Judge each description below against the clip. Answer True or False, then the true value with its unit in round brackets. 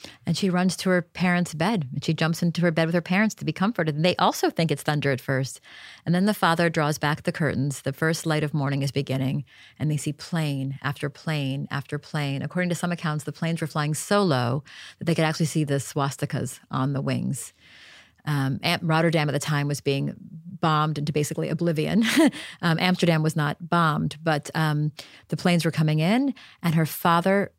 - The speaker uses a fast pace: True (210 wpm)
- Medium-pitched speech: True (155 Hz)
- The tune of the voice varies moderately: True (3.1 semitones)